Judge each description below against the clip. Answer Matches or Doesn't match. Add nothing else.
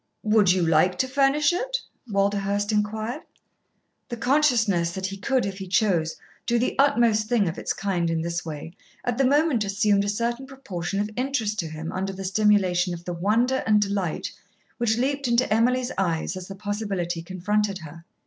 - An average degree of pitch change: Matches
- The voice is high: Matches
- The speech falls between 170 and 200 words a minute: Matches